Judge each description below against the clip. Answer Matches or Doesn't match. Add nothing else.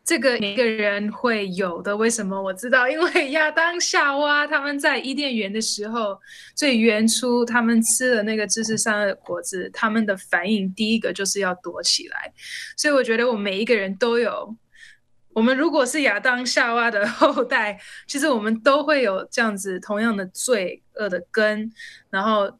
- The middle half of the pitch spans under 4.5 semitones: Doesn't match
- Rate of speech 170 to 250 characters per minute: Doesn't match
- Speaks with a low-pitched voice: Doesn't match